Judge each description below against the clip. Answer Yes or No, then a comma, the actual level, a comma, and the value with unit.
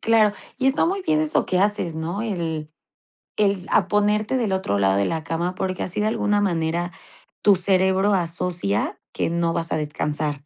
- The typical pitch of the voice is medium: Yes, medium, 180 Hz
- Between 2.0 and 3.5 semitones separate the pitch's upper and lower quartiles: No, average, 4.4 semitones